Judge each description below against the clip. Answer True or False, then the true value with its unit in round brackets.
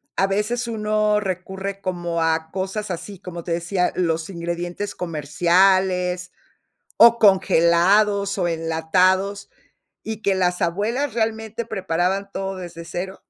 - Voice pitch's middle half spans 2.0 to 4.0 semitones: True (2.8 semitones)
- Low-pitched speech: False (190 Hz)